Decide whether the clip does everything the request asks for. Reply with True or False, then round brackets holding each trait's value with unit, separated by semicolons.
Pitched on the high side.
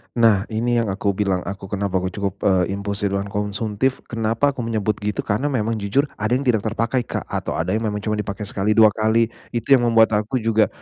False (105 Hz)